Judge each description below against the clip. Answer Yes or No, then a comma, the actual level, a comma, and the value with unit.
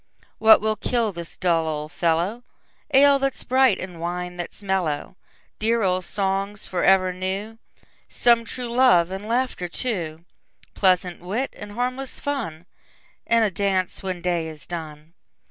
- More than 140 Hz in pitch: Yes, high, 190 Hz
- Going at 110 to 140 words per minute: Yes, slow, 135 wpm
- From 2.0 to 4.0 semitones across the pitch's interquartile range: No, average, 4.9 semitones